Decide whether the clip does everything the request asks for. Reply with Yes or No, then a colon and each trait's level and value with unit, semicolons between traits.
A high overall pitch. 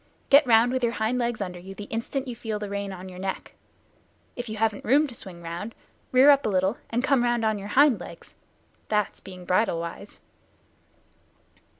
Yes: high, 220 Hz